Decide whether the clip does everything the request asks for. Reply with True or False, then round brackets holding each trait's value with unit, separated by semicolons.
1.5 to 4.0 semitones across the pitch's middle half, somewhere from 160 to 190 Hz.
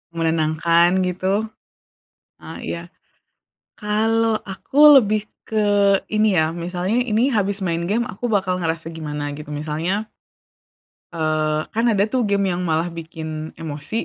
False (4.8 semitones; 185 Hz)